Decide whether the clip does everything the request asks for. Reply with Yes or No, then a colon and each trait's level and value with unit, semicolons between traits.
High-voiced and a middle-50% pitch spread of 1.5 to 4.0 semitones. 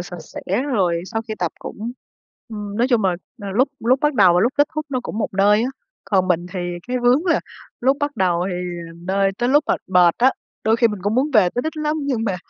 No: high, 225 Hz; wide, 5.4 semitones